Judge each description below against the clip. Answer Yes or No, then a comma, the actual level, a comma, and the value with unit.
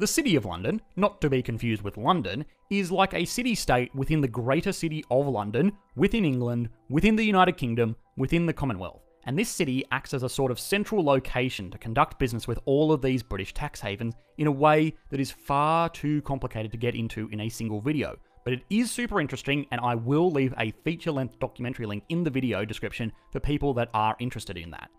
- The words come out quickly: Yes, fast, 215 wpm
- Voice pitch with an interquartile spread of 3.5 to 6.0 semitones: Yes, wide, 5.4 semitones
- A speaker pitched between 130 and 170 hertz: Yes, low, 135 Hz